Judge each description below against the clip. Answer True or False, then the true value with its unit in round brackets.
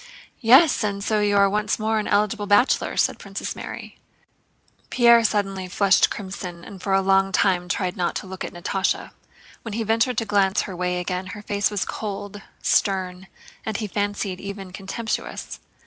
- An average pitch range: False (2.0 semitones)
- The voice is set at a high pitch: True (200 Hz)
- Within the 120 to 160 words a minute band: False (175 wpm)